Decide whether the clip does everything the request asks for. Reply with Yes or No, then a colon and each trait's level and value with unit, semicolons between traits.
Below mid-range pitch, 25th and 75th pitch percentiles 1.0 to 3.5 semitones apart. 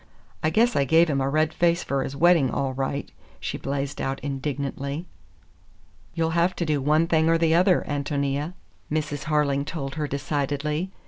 No: medium, 150 Hz; average, 2.8 semitones